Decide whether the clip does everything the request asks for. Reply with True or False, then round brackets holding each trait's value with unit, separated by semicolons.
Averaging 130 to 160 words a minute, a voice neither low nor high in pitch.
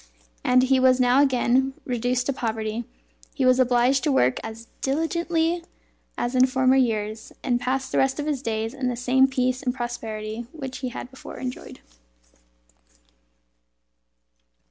False (150 wpm; 255 Hz)